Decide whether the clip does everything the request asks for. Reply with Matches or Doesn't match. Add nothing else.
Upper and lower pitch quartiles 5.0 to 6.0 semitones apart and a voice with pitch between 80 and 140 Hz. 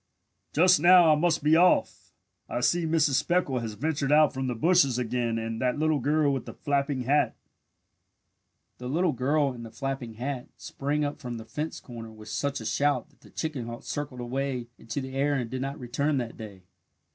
Doesn't match